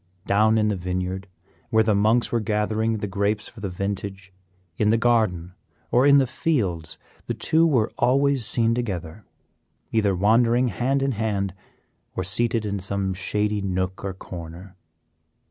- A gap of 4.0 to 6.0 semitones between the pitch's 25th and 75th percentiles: No, average, 3.4 semitones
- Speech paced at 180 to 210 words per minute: No, average, 155 wpm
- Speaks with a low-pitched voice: Yes, low, 105 Hz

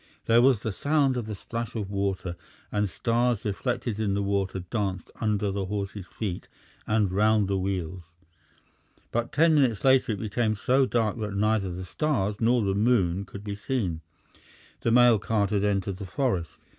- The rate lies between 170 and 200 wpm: Yes, average, 175 wpm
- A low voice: Yes, low, 105 Hz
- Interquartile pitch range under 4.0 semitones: Yes, average, 3.2 semitones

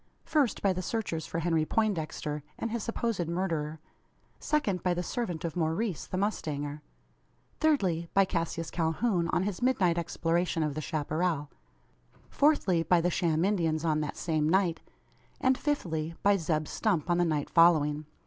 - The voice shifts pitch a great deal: No, average, 3.9 semitones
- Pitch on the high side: No, medium, 170 Hz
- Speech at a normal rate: Yes, average, 160 wpm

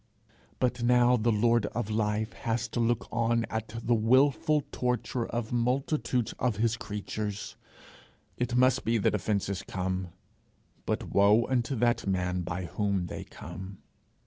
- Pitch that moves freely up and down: No, average, 3.0 semitones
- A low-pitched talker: Yes, low, 115 Hz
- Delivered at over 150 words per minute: No, average, 145 wpm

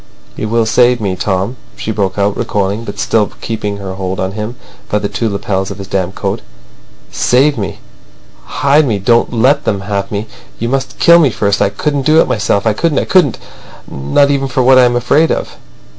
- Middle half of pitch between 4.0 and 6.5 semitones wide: Yes, average, 4.6 semitones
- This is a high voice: No, low, 110 Hz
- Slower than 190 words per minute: No, average, 200 wpm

